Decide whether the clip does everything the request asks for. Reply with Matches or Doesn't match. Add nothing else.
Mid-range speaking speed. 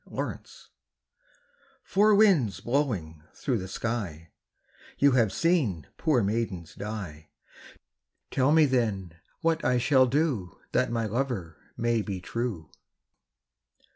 Doesn't match